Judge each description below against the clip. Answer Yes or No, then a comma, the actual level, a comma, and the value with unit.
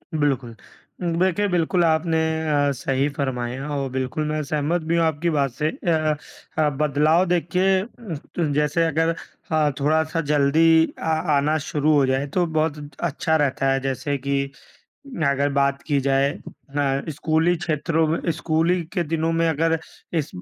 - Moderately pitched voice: Yes, medium, 155 Hz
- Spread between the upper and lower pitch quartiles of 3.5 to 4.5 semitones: No, average, 2.7 semitones